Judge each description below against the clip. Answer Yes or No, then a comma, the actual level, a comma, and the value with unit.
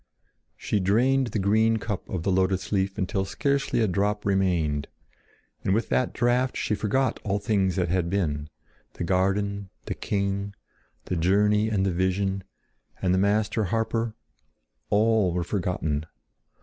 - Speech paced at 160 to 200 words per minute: No, average, 140 wpm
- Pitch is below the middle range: Yes, low, 100 Hz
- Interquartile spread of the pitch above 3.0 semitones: No, average, 2.7 semitones